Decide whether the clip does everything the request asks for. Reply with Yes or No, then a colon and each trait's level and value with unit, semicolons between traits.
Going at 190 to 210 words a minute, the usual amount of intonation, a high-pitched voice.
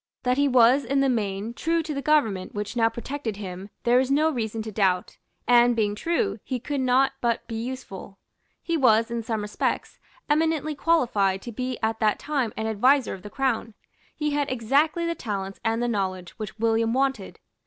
Yes: average, 195 wpm; average, 4.3 semitones; high, 235 Hz